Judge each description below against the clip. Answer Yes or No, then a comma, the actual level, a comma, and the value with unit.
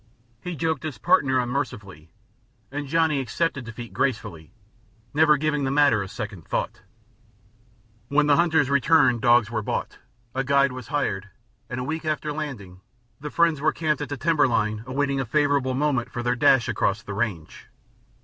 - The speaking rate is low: No, average, 165 wpm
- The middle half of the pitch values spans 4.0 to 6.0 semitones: Yes, average, 4.3 semitones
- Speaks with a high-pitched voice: No, low, 135 Hz